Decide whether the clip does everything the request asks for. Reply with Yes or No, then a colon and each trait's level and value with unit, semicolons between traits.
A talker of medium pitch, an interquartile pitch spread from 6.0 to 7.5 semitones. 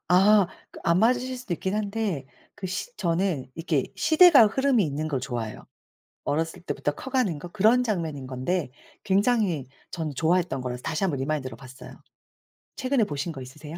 Yes: medium, 175 Hz; wide, 6.8 semitones